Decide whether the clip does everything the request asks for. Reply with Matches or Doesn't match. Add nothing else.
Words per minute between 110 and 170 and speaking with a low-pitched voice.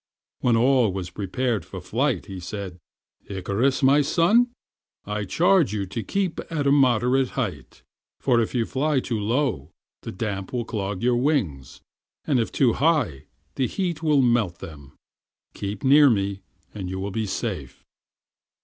Matches